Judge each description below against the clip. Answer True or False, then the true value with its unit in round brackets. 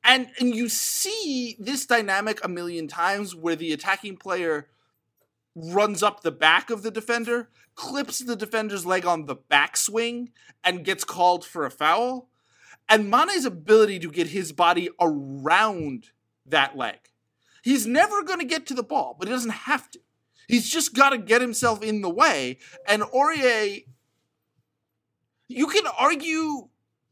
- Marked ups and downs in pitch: True (6.5 semitones)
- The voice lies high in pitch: True (220 Hz)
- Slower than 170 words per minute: True (150 wpm)